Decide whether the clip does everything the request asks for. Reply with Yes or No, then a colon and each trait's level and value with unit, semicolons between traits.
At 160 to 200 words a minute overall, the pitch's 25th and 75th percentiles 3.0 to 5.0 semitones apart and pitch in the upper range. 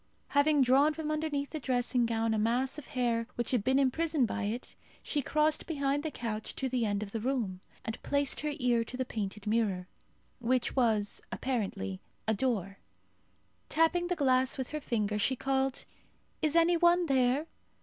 Yes: average, 180 wpm; average, 4.4 semitones; very high, 255 Hz